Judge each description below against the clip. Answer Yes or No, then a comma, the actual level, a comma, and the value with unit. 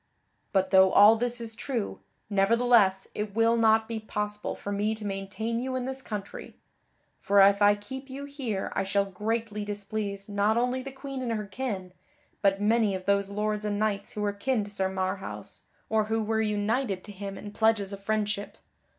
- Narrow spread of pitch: Yes, narrow, 2.2 semitones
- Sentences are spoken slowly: No, average, 190 wpm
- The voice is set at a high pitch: Yes, high, 210 Hz